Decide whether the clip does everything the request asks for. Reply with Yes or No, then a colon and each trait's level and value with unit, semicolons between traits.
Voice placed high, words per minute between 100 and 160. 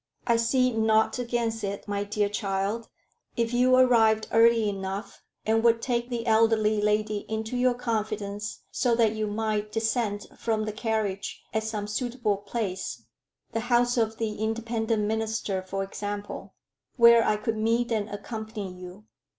Yes: high, 220 Hz; average, 150 wpm